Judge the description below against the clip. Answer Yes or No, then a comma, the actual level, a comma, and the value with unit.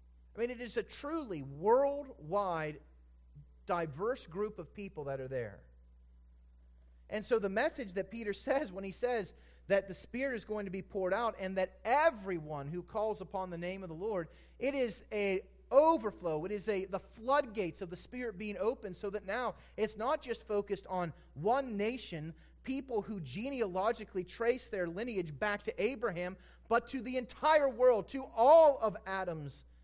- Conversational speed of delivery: Yes, average, 175 wpm